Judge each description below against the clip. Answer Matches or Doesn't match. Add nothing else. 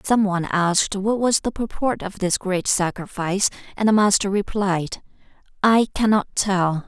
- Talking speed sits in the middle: Matches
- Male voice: Doesn't match